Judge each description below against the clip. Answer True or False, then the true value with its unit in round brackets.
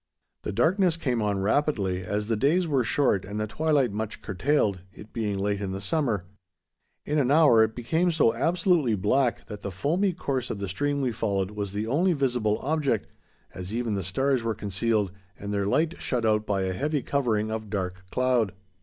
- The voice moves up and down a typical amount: False (5.8 semitones)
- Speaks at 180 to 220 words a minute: True (195 wpm)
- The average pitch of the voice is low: True (115 Hz)